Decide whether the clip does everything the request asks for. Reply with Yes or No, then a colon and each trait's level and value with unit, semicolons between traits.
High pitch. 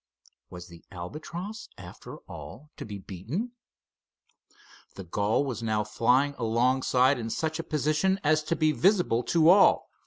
No: low, 130 Hz